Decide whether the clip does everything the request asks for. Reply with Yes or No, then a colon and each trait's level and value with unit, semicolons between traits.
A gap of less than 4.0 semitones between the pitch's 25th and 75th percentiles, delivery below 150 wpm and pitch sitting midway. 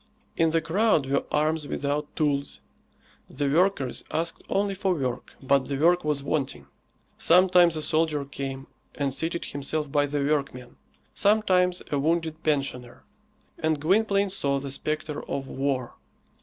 Yes: average, 3.4 semitones; average, 140 wpm; medium, 150 Hz